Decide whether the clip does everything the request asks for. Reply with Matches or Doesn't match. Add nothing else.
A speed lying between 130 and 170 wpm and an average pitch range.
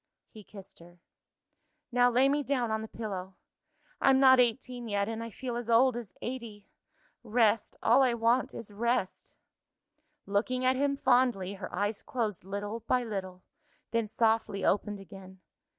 Matches